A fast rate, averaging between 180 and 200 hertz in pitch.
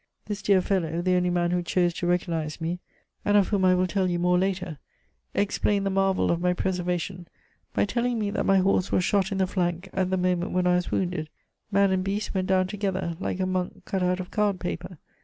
Yes: fast, 230 wpm; medium, 185 Hz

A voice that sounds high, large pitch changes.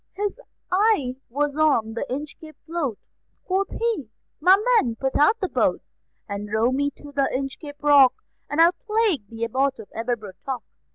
Yes: very high, 285 Hz; wide, 5.8 semitones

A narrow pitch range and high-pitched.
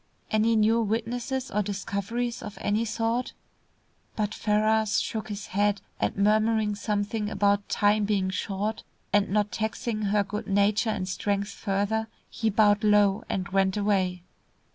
Yes: narrow, 1.5 semitones; high, 210 Hz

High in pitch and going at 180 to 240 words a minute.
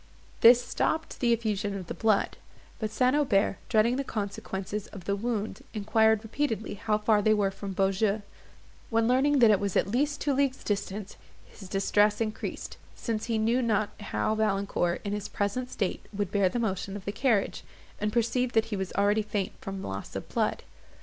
Yes: high, 210 Hz; average, 185 wpm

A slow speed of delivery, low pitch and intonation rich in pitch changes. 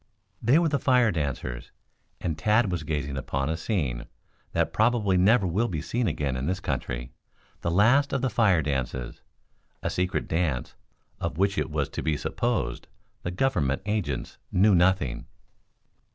No: average, 160 wpm; very low, 90 Hz; wide, 7.1 semitones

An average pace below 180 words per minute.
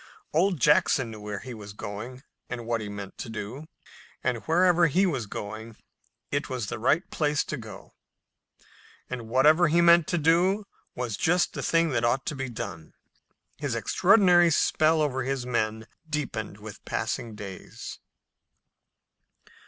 Yes: average, 160 wpm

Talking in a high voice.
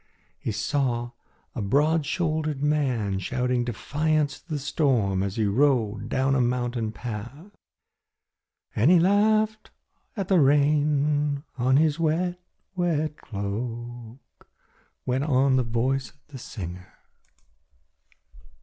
No: low, 135 Hz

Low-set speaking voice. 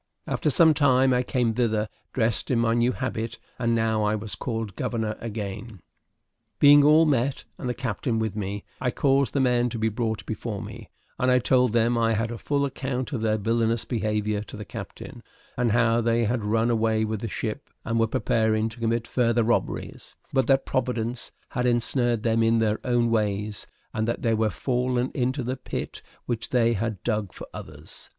Yes: low, 115 Hz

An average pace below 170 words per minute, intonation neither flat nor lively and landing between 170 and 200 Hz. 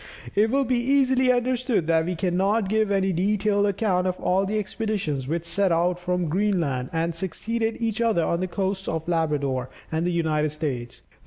No: average, 180 wpm; average, 4.6 semitones; medium, 185 Hz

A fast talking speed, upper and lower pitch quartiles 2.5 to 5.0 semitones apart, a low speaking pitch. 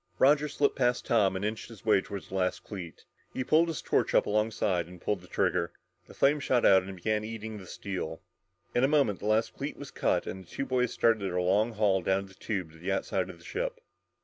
Yes: fast, 235 wpm; average, 4.2 semitones; low, 105 Hz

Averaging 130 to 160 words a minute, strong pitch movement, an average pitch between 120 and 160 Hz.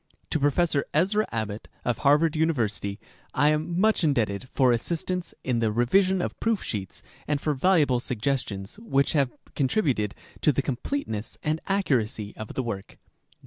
Yes: average, 150 wpm; wide, 6.4 semitones; medium, 140 Hz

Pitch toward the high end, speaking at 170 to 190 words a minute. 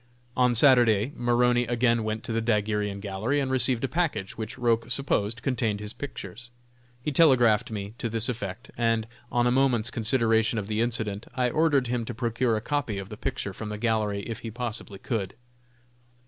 No: low, 115 Hz; average, 185 wpm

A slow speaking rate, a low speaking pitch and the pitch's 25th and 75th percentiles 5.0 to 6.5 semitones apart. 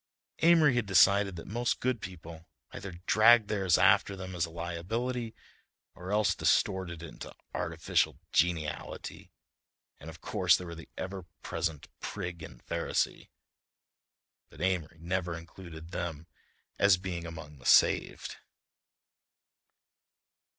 No: slow, 120 wpm; very low, 90 Hz; average, 3.1 semitones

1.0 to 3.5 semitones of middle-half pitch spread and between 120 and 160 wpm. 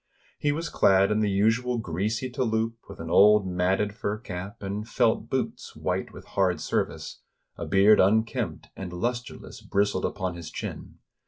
No: average, 3.0 semitones; average, 170 wpm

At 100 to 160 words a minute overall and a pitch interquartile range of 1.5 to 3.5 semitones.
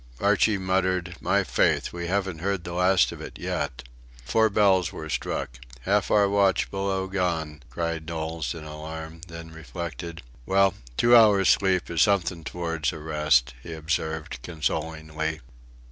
Yes: average, 145 wpm; average, 3.2 semitones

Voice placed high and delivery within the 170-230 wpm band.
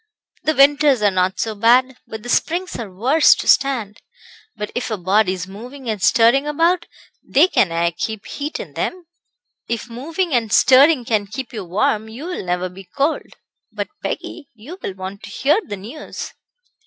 Yes: high, 235 Hz; average, 180 wpm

